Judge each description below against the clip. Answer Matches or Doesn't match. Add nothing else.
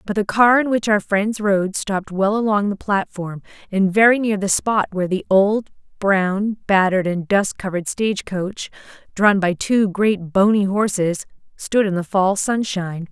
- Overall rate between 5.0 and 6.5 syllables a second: Doesn't match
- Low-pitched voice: Doesn't match